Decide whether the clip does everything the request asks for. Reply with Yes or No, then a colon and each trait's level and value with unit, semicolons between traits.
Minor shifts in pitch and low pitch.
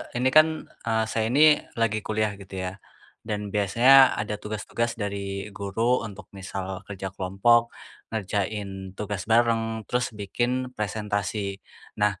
Yes: narrow, 2.3 semitones; low, 105 Hz